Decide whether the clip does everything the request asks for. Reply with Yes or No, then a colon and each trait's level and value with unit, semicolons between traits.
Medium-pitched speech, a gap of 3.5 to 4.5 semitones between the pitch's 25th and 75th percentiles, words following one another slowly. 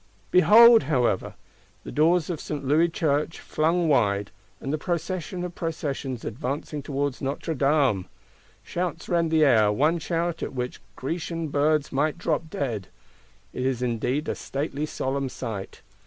No: medium, 150 Hz; average, 3.9 semitones; average, 145 wpm